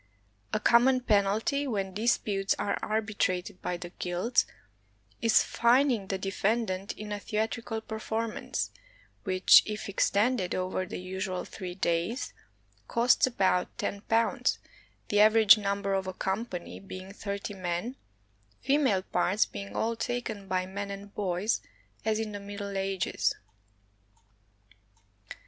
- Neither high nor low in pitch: No, high, 200 Hz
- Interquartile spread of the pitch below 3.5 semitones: Yes, average, 2.9 semitones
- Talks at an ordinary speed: No, slow, 125 wpm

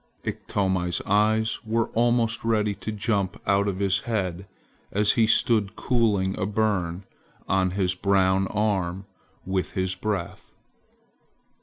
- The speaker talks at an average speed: No, slow, 125 wpm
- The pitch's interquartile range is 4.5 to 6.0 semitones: No, narrow, 2.5 semitones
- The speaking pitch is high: No, low, 100 Hz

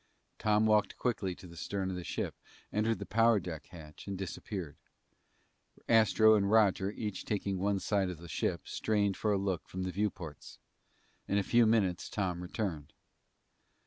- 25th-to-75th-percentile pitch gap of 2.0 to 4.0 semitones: Yes, average, 2.9 semitones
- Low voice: Yes, low, 100 Hz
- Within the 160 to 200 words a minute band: Yes, average, 170 wpm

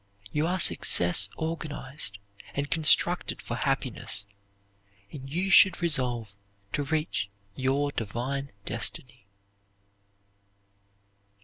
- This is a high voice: No, medium, 140 Hz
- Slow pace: Yes, slow, 90 wpm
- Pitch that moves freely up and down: No, average, 4.9 semitones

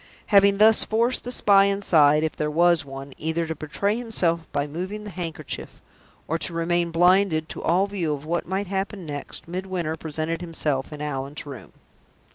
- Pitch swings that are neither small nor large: Yes, average, 4.2 semitones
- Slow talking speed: No, average, 175 wpm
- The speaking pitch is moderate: Yes, medium, 170 Hz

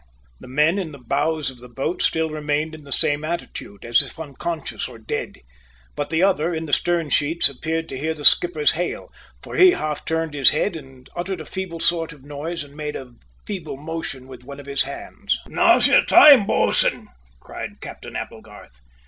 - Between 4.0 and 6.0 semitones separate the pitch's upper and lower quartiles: No, average, 3.0 semitones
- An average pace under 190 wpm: No, average, 195 wpm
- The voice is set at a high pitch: No, medium, 155 Hz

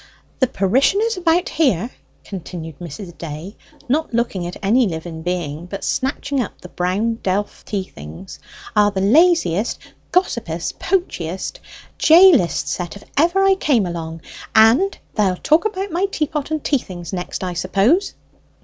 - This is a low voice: No, high, 205 Hz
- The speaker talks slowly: No, average, 150 wpm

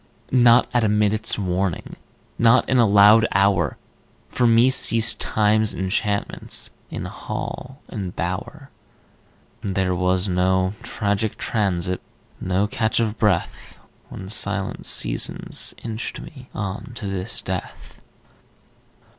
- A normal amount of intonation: Yes, average, 3.3 semitones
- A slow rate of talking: Yes, slow, 115 wpm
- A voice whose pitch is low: Yes, low, 105 Hz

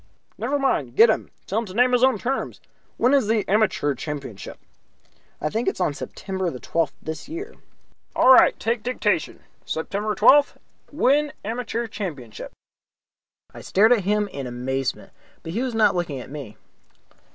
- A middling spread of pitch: No, wide, 8.0 semitones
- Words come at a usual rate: Yes, average, 165 wpm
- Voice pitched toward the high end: Yes, high, 210 Hz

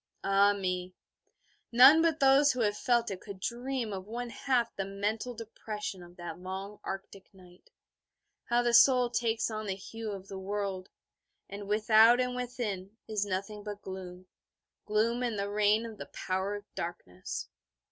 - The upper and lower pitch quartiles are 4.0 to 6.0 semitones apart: No, average, 3.5 semitones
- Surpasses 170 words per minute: No, average, 165 wpm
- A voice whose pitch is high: Yes, high, 210 Hz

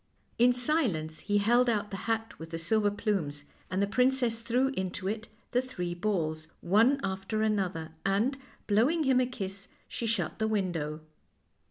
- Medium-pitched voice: No, high, 210 Hz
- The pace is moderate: Yes, average, 165 wpm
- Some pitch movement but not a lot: Yes, average, 4.7 semitones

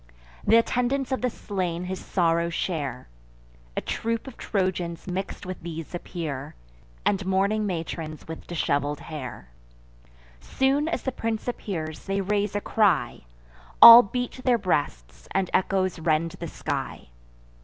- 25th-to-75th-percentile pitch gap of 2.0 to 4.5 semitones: No, average, 4.9 semitones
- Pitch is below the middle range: No, medium, 185 Hz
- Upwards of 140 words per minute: No, slow, 135 wpm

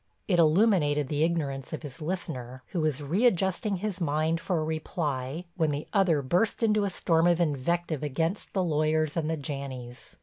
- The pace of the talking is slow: No, average, 175 wpm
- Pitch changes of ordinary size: Yes, average, 3.3 semitones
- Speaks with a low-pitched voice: No, medium, 160 Hz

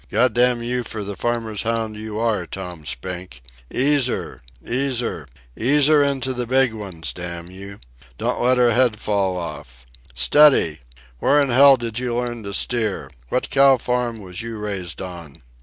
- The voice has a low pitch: Yes, low, 115 Hz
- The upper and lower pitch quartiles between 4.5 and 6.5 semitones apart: Yes, average, 5.0 semitones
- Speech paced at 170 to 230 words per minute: Yes, average, 175 wpm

